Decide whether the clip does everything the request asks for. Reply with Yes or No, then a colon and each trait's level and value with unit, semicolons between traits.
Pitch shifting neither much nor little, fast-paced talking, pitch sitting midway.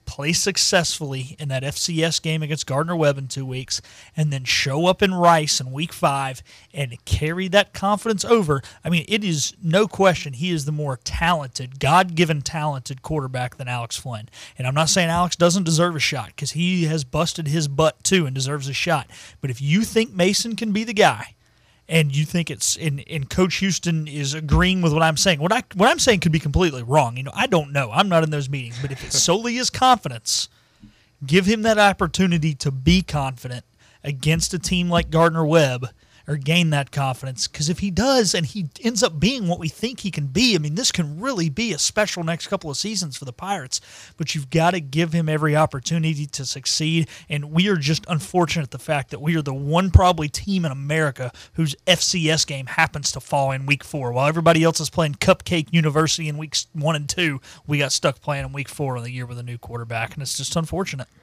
Yes: average, 4.1 semitones; fast, 220 wpm; medium, 155 Hz